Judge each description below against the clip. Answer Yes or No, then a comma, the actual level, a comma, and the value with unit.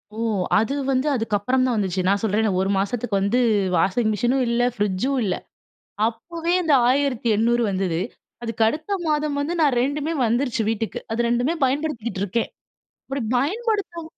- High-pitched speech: Yes, high, 240 Hz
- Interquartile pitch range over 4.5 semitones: Yes, average, 4.9 semitones